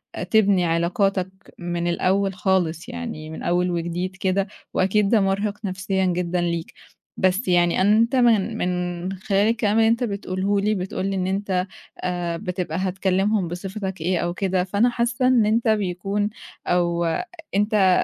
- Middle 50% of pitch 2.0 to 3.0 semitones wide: Yes, narrow, 2.5 semitones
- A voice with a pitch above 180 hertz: Yes, high, 190 Hz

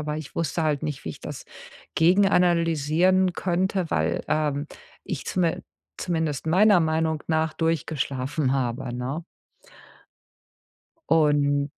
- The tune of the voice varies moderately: Yes, average, 3.0 semitones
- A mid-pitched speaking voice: Yes, medium, 160 Hz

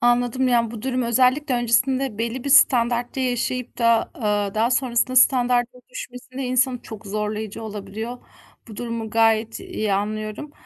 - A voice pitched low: No, high, 240 Hz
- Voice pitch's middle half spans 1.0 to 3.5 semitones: Yes, narrow, 2.5 semitones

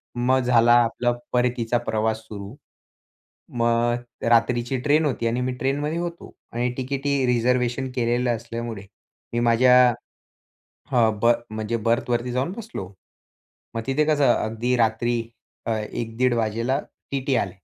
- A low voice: Yes, low, 120 Hz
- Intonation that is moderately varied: No, narrow, 1.7 semitones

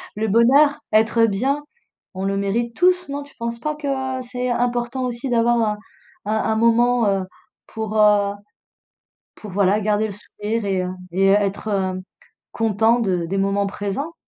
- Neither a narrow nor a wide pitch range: Yes, average, 3.2 semitones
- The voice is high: Yes, high, 220 Hz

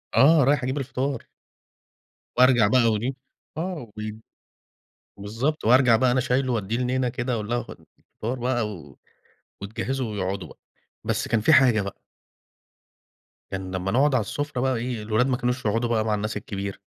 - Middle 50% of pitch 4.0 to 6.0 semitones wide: No, average, 3.3 semitones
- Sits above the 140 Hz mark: No, low, 120 Hz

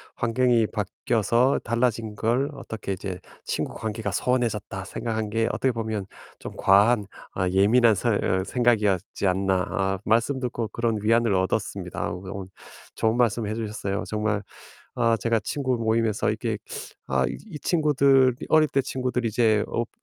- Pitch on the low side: Yes, low, 115 Hz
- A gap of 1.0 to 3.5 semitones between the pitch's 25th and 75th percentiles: Yes, average, 3.0 semitones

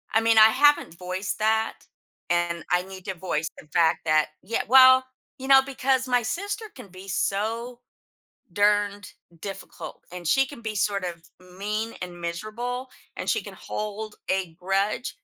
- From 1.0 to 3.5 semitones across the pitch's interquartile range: No, average, 4.9 semitones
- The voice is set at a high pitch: Yes, high, 205 Hz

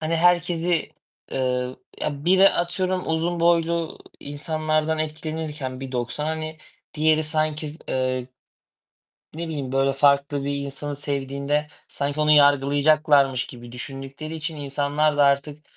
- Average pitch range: No, narrow, 2.3 semitones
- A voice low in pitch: No, medium, 150 Hz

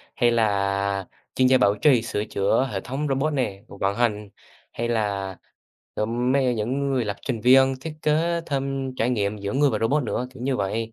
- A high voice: No, low, 120 Hz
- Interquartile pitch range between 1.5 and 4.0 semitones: No, average, 4.6 semitones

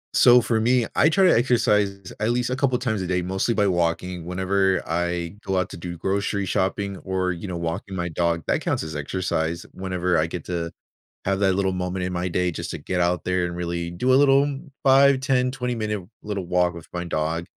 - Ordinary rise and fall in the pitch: Yes, average, 3.9 semitones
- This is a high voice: No, very low, 95 Hz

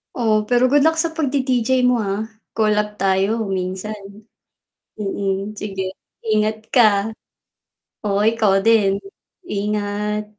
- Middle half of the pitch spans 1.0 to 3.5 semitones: Yes, average, 2.8 semitones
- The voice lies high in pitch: Yes, high, 210 Hz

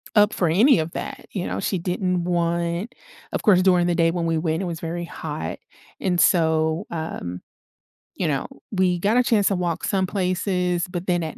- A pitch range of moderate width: No, narrow, 2.1 semitones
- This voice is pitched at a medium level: Yes, medium, 175 Hz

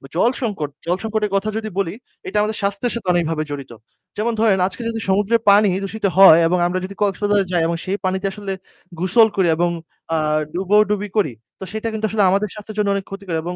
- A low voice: No, high, 200 Hz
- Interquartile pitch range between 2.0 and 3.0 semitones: Yes, average, 2.7 semitones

